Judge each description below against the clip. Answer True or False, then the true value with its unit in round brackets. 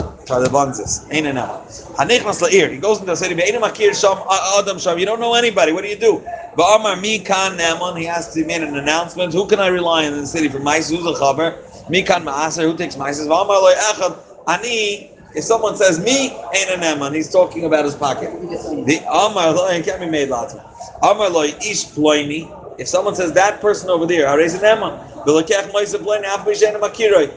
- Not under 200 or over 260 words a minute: True (205 wpm)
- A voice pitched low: False (180 Hz)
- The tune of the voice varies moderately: True (4.9 semitones)